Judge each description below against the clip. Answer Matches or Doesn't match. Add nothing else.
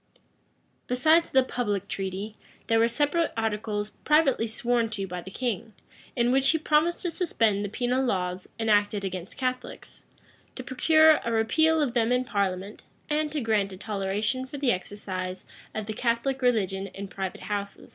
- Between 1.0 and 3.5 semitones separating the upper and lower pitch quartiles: Doesn't match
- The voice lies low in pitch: Doesn't match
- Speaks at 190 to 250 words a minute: Doesn't match